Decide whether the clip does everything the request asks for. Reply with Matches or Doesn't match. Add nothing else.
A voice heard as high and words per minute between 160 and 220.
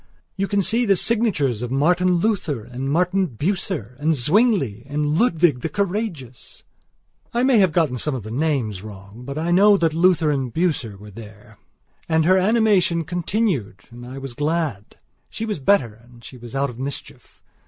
Doesn't match